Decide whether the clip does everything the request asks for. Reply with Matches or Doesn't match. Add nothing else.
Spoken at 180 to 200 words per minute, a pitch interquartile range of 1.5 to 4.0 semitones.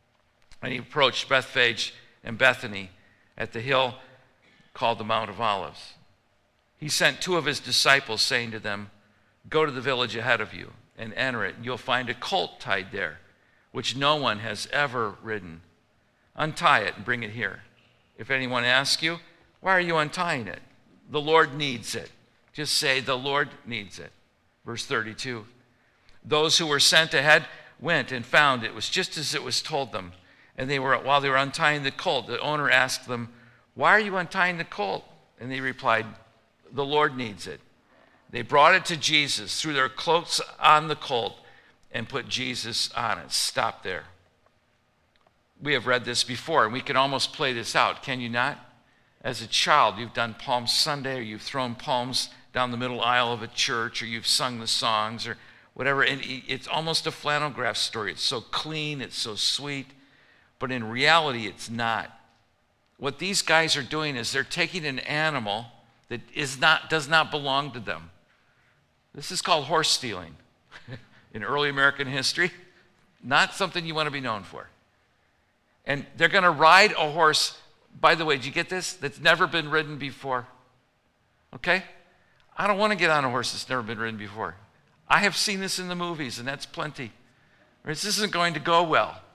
Doesn't match